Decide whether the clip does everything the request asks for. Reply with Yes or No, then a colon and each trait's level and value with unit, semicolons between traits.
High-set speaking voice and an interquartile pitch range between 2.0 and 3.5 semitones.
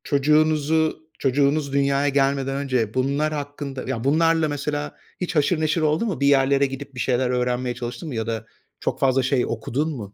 No: medium, 140 Hz; average, 2.8 semitones